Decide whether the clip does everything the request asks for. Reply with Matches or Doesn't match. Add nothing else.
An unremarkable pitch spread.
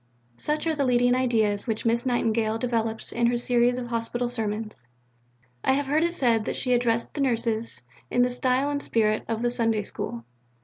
Doesn't match